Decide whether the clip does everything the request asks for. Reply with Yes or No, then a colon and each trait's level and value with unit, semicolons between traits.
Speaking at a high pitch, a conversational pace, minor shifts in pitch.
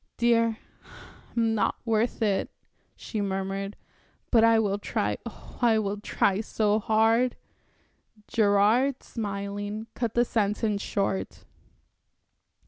No: high, 215 Hz; slow, 110 wpm; narrow, 2.1 semitones